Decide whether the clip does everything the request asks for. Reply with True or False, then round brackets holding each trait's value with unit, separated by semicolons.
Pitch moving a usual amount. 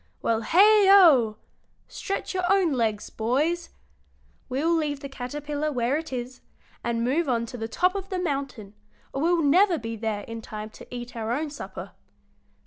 False (6.4 semitones)